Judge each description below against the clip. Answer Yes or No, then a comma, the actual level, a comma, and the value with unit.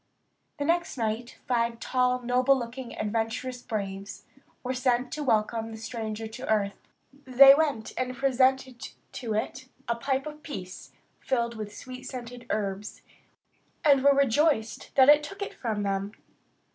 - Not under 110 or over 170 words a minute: Yes, average, 145 wpm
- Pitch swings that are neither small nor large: Yes, average, 3.3 semitones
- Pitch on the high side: Yes, high, 245 Hz